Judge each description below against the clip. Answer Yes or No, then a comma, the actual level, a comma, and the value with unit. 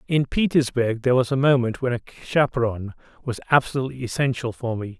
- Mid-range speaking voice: No, low, 125 Hz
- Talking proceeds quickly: No, average, 170 wpm